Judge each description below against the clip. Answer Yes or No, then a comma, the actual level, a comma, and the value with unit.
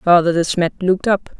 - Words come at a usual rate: No, fast, 215 wpm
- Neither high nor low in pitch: Yes, medium, 180 Hz